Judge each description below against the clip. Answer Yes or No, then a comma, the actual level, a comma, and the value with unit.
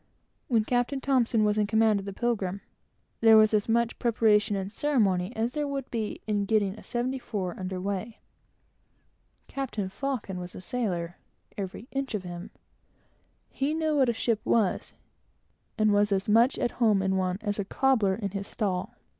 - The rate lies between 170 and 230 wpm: Yes, average, 175 wpm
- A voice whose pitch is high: Yes, high, 215 Hz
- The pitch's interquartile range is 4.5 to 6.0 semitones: No, average, 3.6 semitones